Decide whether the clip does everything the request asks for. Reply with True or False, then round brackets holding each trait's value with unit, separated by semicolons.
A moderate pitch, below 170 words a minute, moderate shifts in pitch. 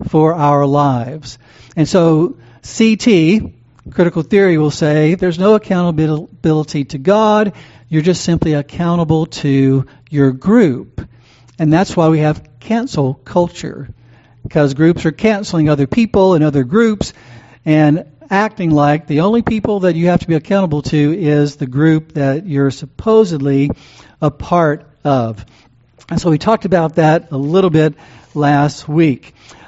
True (155 Hz; 145 wpm; 4.0 semitones)